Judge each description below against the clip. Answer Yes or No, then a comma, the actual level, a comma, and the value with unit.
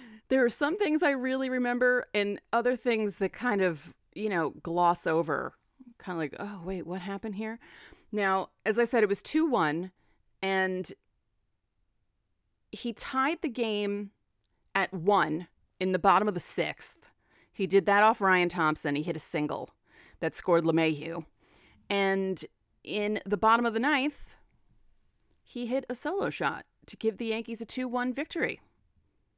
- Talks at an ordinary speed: Yes, average, 160 wpm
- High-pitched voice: Yes, high, 205 Hz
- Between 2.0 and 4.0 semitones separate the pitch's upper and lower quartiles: No, average, 5.3 semitones